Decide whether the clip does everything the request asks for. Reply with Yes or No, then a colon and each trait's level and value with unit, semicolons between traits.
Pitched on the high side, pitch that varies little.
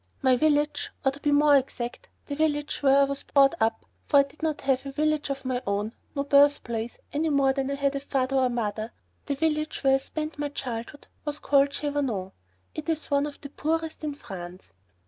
Yes: very high, 280 Hz; narrow, 2.1 semitones